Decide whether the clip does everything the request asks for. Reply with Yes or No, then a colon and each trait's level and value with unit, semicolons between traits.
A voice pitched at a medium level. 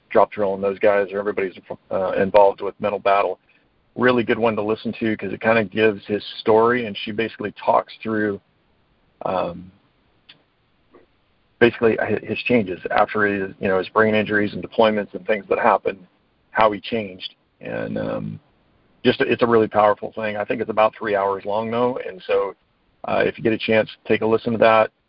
No: low, 110 Hz